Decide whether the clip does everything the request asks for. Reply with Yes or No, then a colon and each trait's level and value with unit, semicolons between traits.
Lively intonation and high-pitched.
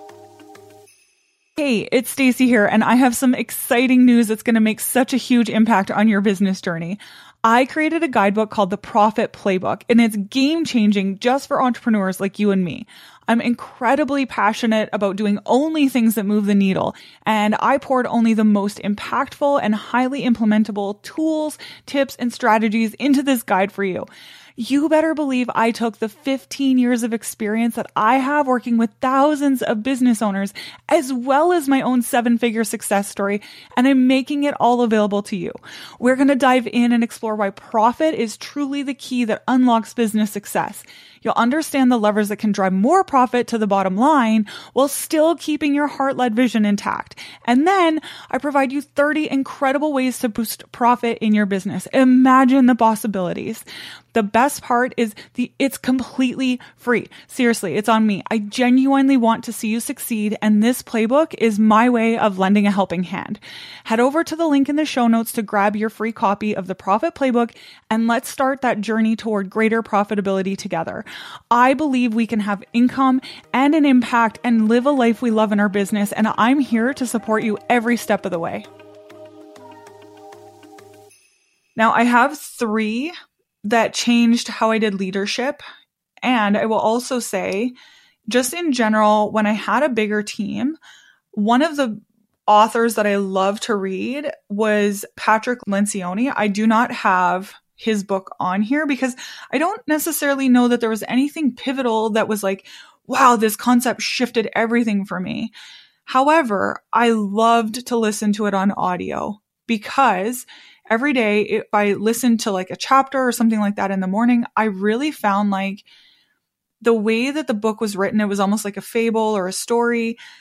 No: average, 3.5 semitones; high, 230 Hz